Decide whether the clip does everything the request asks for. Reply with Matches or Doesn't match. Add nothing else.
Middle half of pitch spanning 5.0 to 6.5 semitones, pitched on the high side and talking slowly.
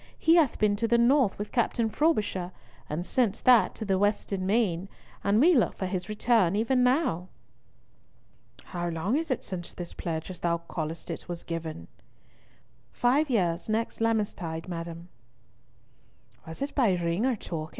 Doesn't match